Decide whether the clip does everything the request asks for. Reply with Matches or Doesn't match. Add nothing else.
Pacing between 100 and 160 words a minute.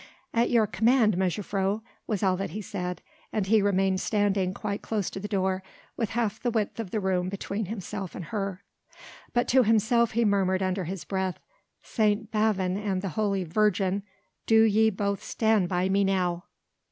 Doesn't match